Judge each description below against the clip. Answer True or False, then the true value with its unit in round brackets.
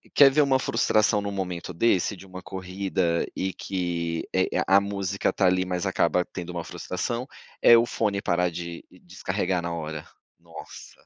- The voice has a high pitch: False (95 Hz)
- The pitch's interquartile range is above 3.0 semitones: False (2.4 semitones)